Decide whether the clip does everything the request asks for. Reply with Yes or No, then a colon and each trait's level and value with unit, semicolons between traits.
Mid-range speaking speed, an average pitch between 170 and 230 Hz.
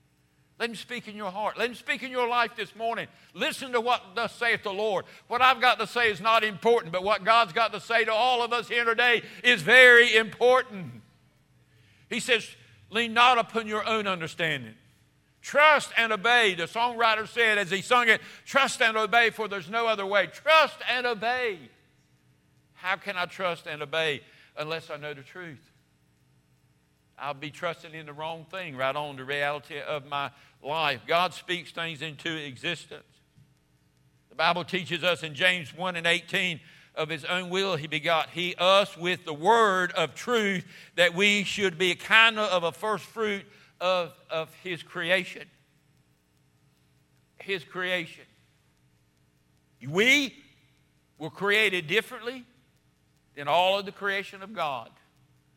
Yes: average, 165 wpm; medium, 185 Hz